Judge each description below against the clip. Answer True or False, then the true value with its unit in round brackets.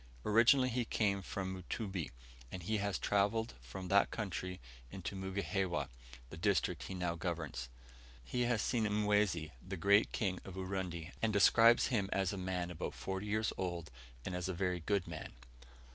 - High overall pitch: False (95 Hz)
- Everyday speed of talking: True (165 wpm)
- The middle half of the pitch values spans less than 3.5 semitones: True (2.6 semitones)